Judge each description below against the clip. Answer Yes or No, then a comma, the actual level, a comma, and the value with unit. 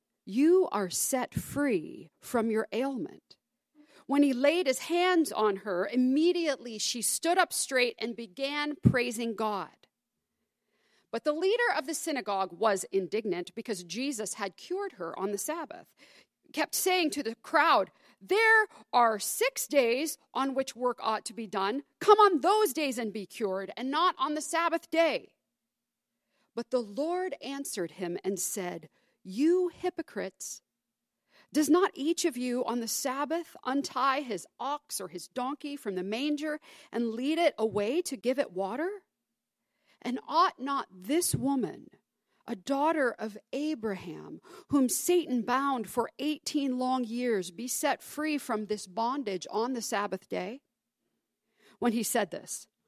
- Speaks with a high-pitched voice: Yes, very high, 255 Hz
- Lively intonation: Yes, wide, 5.7 semitones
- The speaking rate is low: No, average, 150 wpm